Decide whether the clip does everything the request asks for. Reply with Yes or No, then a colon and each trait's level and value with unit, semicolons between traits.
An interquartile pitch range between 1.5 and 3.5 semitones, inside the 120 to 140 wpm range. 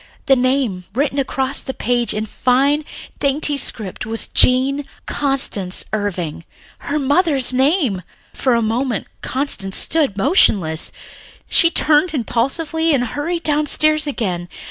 No: average, 5.0 semitones; slow, 135 wpm